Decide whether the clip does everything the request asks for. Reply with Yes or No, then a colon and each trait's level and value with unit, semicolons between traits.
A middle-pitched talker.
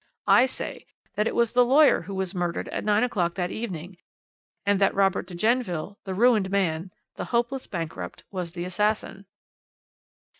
No: high, 195 Hz